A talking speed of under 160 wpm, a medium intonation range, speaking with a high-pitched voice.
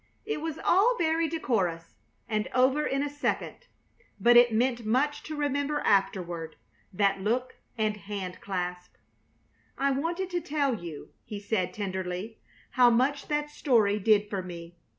No: average, 150 wpm; wide, 7.0 semitones; high, 230 Hz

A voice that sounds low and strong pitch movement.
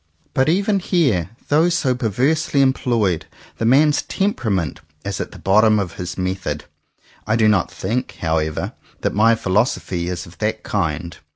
Yes: low, 110 Hz; wide, 6.5 semitones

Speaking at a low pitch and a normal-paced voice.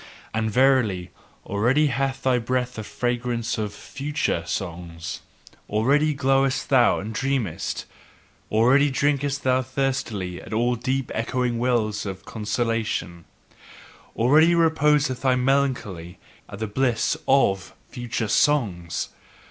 No: low, 125 Hz; slow, 115 wpm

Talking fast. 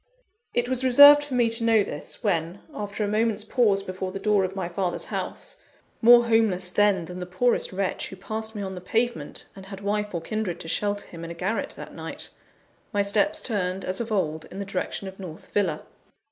Yes: fast, 215 wpm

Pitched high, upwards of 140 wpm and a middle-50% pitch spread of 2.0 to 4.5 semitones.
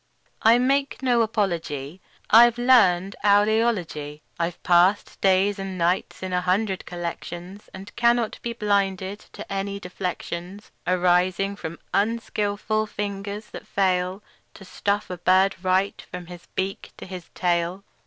No: high, 195 Hz; slow, 135 wpm; narrow, 2.6 semitones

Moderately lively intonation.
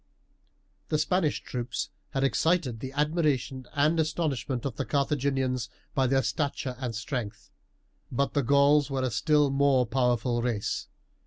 Yes: average, 3.0 semitones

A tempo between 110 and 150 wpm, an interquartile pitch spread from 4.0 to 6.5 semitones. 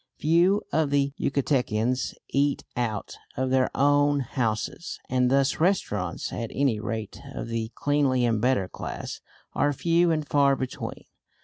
No: average, 140 wpm; average, 3.6 semitones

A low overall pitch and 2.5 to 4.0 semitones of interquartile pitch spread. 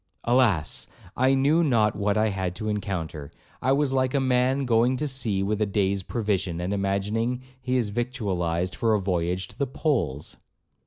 No: low, 110 Hz; average, 5.0 semitones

